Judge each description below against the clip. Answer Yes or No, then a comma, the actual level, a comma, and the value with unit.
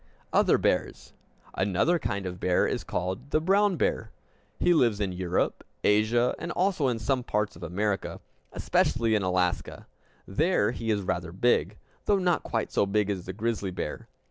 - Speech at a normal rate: Yes, average, 170 wpm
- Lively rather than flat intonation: Yes, wide, 5.7 semitones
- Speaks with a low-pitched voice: Yes, low, 105 Hz